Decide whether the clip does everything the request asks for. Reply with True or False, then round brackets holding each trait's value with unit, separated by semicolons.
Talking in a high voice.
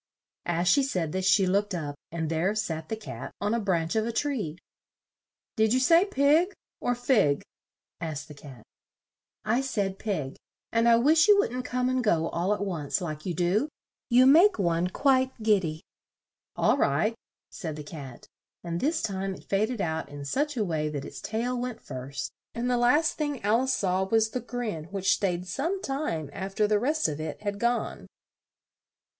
True (205 Hz)